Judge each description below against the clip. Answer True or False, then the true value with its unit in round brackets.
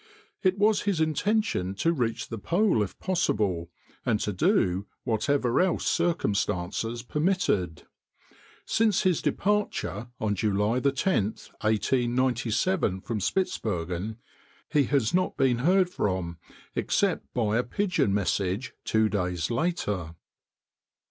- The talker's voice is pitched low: True (115 Hz)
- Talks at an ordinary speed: False (115 wpm)